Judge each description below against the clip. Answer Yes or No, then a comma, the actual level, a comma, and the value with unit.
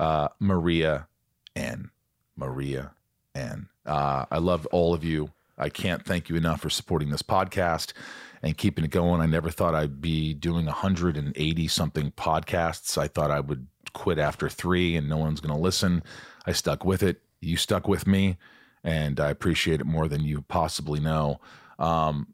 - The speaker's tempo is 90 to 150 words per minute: No, average, 170 wpm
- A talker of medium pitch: No, very low, 80 Hz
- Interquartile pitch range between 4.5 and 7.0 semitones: No, narrow, 2.6 semitones